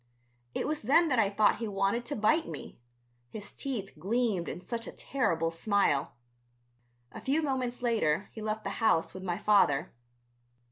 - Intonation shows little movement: No, average, 4.5 semitones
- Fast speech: No, average, 170 wpm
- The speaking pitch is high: Yes, high, 215 Hz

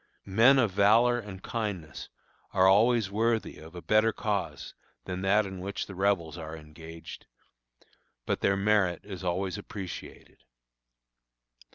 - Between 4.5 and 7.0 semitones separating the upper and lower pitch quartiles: No, average, 3.2 semitones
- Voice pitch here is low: Yes, low, 100 Hz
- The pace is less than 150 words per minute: Yes, slow, 135 wpm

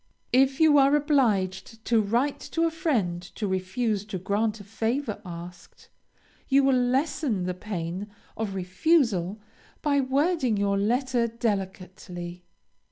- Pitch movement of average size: No, wide, 6.1 semitones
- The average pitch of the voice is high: Yes, high, 220 Hz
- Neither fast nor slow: No, slow, 130 wpm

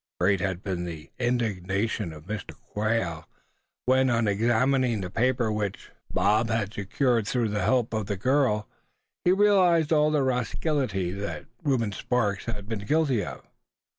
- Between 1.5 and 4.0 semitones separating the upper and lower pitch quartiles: No, average, 4.5 semitones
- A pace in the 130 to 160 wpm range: Yes, average, 150 wpm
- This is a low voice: Yes, low, 110 Hz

